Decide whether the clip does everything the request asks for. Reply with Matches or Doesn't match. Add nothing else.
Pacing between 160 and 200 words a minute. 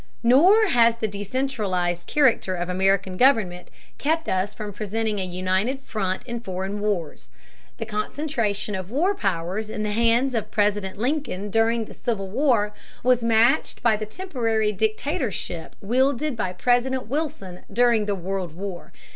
Doesn't match